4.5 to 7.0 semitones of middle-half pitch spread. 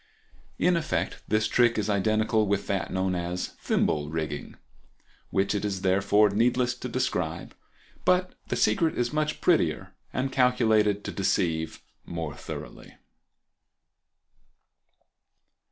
Yes: average, 5.3 semitones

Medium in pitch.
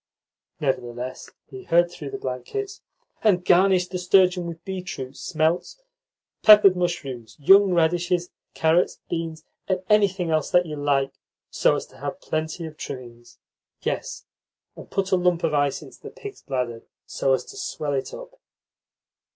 Yes: medium, 170 Hz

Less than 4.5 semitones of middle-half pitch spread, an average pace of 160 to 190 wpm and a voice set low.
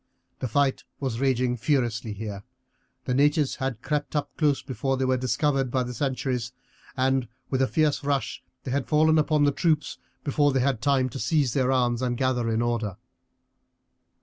Yes: narrow, 2.6 semitones; average, 175 wpm; low, 130 Hz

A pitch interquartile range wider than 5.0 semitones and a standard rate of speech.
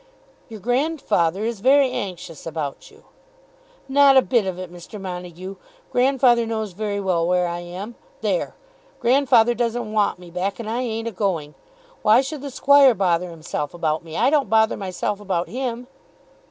Yes: wide, 5.4 semitones; average, 165 wpm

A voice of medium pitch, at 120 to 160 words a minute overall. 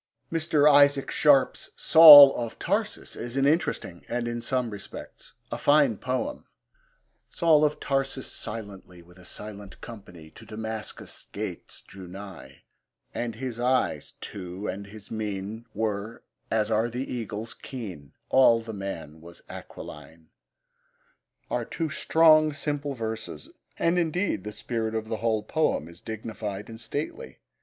No: low, 115 Hz; average, 140 wpm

